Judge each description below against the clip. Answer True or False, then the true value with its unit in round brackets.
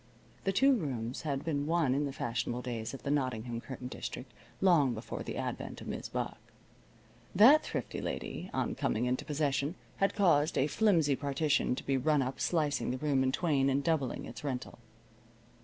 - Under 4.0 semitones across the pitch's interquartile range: True (3.5 semitones)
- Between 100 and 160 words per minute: False (180 wpm)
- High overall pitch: False (140 Hz)